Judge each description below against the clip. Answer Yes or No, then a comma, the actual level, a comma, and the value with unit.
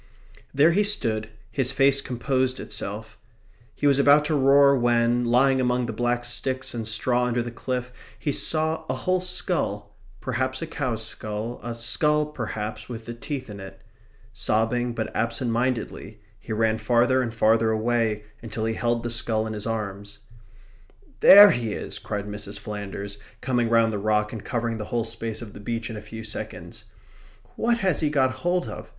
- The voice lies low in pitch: Yes, low, 120 Hz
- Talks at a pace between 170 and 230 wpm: Yes, average, 180 wpm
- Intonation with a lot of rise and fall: No, average, 3.0 semitones